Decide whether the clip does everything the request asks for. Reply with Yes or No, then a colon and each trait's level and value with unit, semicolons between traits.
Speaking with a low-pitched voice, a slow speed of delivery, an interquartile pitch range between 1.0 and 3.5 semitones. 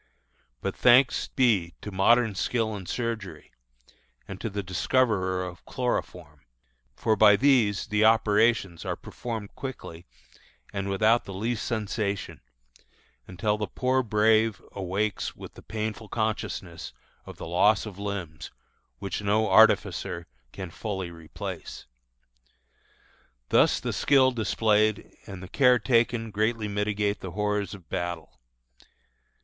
Yes: low, 105 Hz; slow, 125 wpm; average, 3.0 semitones